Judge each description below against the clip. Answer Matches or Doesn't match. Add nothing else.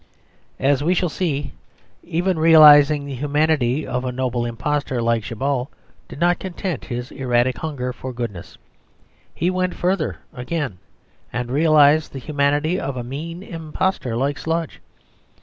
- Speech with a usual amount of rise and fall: Matches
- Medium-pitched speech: Matches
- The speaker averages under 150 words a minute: Matches